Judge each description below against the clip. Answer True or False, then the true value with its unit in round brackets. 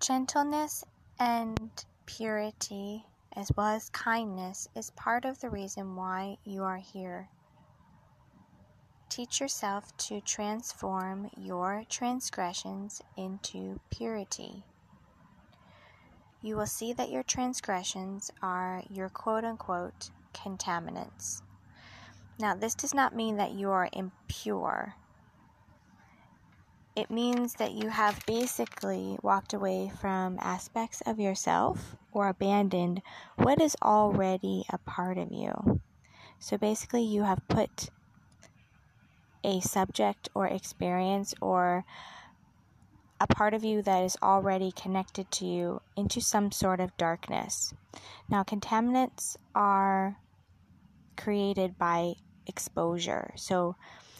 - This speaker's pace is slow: True (105 wpm)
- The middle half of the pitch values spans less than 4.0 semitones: True (3.1 semitones)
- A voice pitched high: True (195 Hz)